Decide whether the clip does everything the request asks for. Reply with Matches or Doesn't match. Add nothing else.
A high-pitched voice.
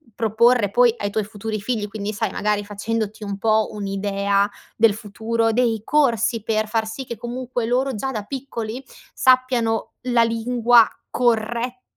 Matches